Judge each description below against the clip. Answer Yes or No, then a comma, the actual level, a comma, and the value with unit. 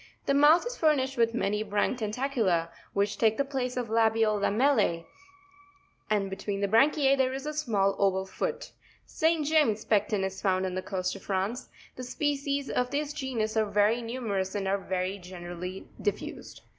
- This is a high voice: Yes, high, 220 Hz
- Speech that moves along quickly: No, average, 180 wpm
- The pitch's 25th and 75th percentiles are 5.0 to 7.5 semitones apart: Yes, wide, 5.6 semitones